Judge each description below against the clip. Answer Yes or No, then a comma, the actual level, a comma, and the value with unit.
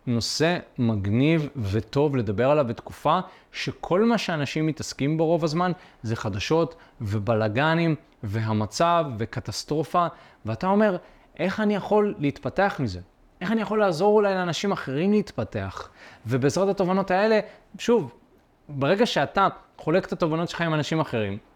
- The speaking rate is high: No, average, 130 wpm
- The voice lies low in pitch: No, medium, 155 Hz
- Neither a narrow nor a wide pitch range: No, wide, 8.0 semitones